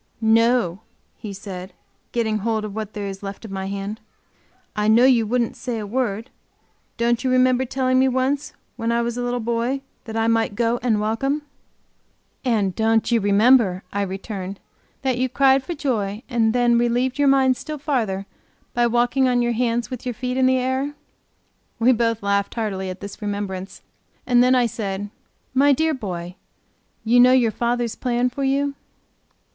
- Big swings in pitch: No, average, 3.5 semitones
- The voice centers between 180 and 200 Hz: No, high, 235 Hz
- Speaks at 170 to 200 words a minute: Yes, average, 180 wpm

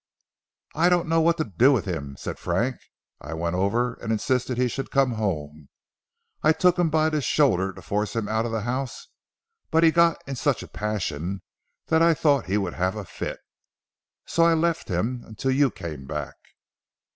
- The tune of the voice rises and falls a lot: Yes, wide, 8.3 semitones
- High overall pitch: No, low, 120 Hz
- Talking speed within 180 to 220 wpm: Yes, average, 190 wpm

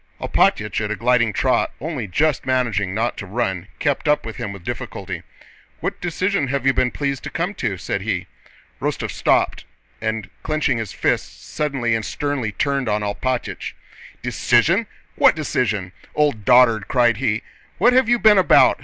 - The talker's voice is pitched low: Yes, low, 125 Hz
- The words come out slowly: No, average, 165 wpm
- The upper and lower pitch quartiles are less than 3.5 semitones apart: No, average, 5.1 semitones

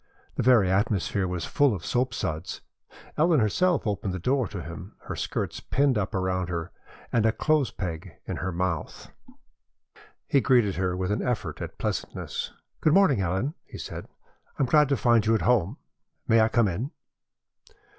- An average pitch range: No, wide, 5.7 semitones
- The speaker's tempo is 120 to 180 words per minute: Yes, average, 175 wpm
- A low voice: Yes, low, 105 Hz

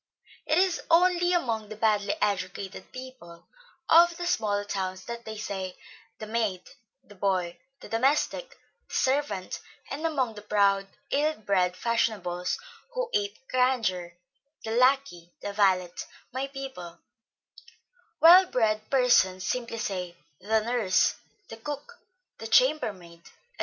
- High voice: Yes, high, 220 Hz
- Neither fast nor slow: No, slow, 130 wpm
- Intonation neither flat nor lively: No, wide, 6.2 semitones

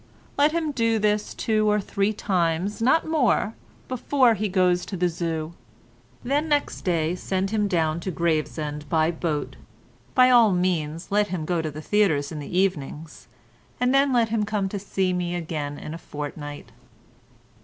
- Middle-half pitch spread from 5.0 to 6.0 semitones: Yes, average, 5.3 semitones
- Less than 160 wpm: No, average, 165 wpm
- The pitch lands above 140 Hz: Yes, medium, 185 Hz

